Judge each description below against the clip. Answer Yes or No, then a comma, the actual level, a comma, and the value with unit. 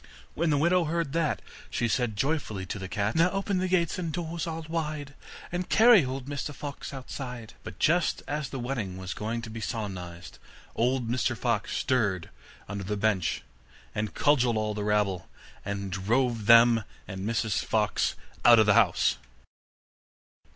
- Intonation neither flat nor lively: No, wide, 6.4 semitones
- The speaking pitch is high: No, low, 120 Hz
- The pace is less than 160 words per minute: No, average, 165 wpm